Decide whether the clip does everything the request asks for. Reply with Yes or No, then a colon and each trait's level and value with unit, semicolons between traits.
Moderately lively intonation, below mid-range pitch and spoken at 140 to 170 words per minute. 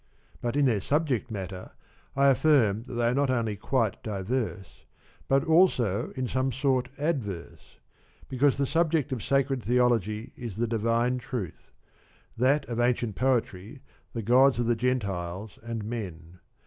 Yes: average, 3.9 semitones; low, 120 Hz; average, 150 wpm